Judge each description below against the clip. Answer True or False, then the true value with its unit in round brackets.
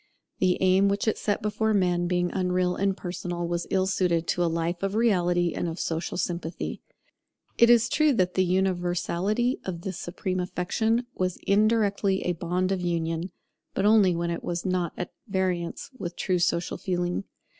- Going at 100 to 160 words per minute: False (175 wpm)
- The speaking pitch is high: False (180 Hz)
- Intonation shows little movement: True (2.1 semitones)